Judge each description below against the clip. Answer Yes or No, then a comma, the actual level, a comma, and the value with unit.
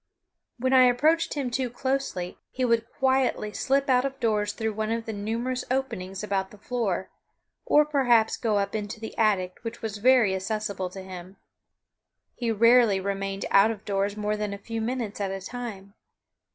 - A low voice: No, high, 220 Hz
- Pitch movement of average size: Yes, average, 3.8 semitones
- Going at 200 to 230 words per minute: No, average, 180 wpm